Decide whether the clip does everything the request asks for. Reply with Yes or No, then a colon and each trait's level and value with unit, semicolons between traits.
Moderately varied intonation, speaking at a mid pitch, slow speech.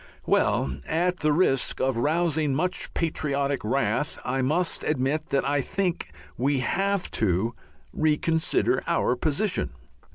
Yes: average, 3.9 semitones; medium, 145 Hz; slow, 125 wpm